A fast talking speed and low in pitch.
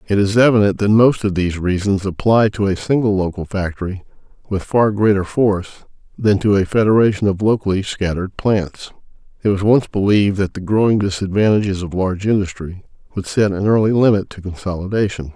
No: average, 170 wpm; low, 100 Hz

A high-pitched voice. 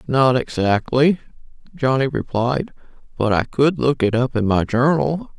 No: low, 130 Hz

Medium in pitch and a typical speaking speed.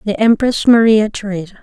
No: high, 215 Hz; average, 145 wpm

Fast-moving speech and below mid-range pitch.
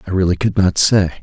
Yes: fast, 245 wpm; very low, 95 Hz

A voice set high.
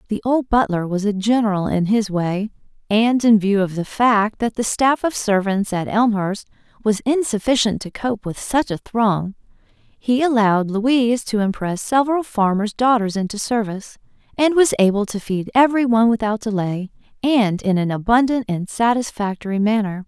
Yes: high, 220 Hz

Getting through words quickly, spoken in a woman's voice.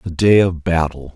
No: fast, 210 wpm; male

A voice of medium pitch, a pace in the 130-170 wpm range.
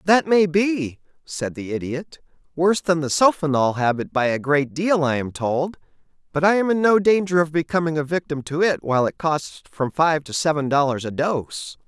No: medium, 155 Hz; average, 200 wpm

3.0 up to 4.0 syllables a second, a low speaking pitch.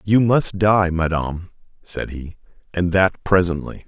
Yes: 3.9 syllables/s; very low, 90 Hz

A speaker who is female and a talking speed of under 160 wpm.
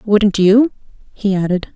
Yes: female; slow, 135 wpm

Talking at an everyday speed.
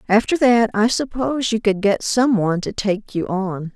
No: fast, 210 wpm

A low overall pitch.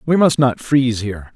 Yes: low, 125 Hz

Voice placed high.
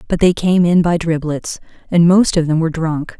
No: medium, 165 Hz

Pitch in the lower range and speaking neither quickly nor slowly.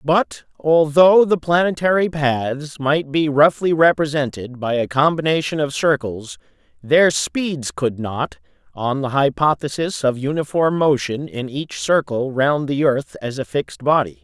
No: medium, 145 Hz; average, 145 wpm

